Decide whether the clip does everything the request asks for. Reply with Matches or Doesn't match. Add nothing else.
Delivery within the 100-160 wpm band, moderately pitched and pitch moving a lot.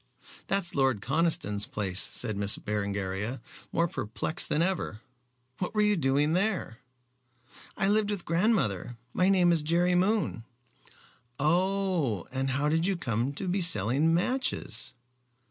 Matches